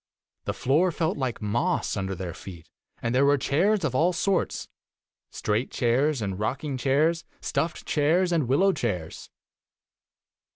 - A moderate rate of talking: Yes, average, 160 wpm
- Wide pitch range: Yes, wide, 6.2 semitones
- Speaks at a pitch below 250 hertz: Yes, low, 135 Hz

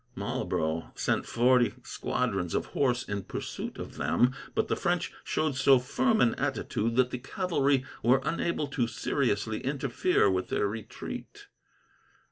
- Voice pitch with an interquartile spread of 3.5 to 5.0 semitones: Yes, average, 4.1 semitones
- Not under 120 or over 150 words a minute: Yes, average, 140 wpm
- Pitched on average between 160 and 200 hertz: No, low, 125 Hz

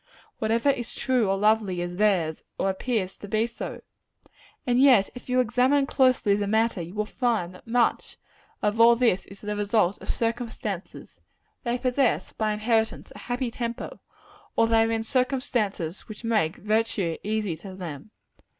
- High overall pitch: Yes, high, 220 Hz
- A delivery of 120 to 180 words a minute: Yes, average, 165 wpm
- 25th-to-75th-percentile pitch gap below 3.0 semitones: No, average, 3.3 semitones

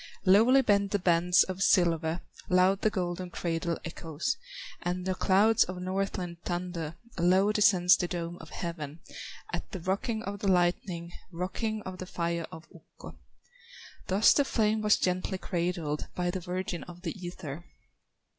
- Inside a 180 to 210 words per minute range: No, average, 155 wpm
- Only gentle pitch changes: Yes, narrow, 2.3 semitones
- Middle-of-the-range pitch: Yes, medium, 180 Hz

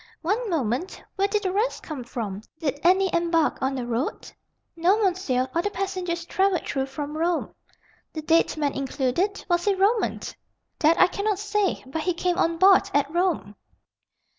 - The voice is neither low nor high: No, very high, 340 Hz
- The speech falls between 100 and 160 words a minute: No, average, 170 wpm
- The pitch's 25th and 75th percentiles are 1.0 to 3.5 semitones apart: No, average, 5.2 semitones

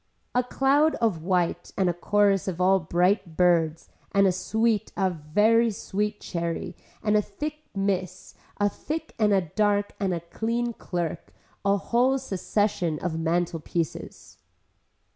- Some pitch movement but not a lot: Yes, average, 3.8 semitones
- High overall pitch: Yes, high, 195 Hz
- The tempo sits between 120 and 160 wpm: Yes, average, 145 wpm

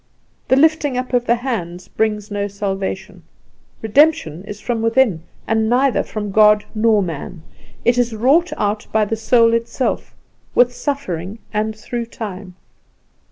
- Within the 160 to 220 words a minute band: No, average, 145 wpm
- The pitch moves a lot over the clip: No, average, 3.2 semitones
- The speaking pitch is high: Yes, high, 220 Hz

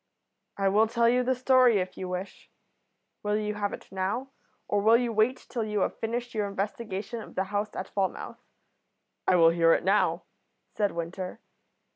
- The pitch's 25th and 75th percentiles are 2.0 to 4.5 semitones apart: Yes, average, 3.4 semitones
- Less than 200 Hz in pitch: No, high, 210 Hz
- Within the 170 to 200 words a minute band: Yes, average, 180 wpm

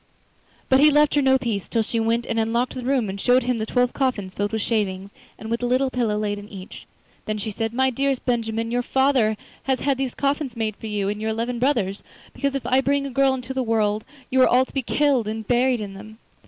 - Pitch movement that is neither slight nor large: Yes, average, 3.4 semitones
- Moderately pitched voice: No, high, 235 Hz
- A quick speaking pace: Yes, fast, 250 wpm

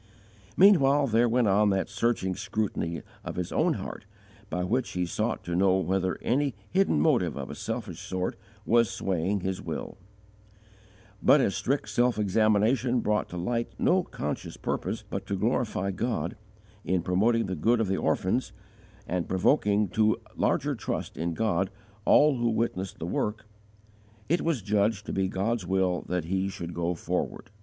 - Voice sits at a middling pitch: No, low, 100 Hz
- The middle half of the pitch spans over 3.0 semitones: Yes, average, 4.1 semitones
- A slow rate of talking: No, average, 165 wpm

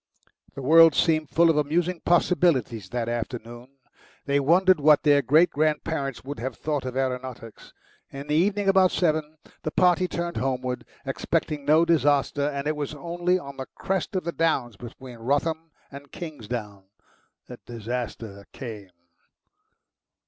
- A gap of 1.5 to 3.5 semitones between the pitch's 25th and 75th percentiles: No, average, 4.7 semitones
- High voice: No, medium, 145 Hz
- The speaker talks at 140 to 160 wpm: Yes, average, 145 wpm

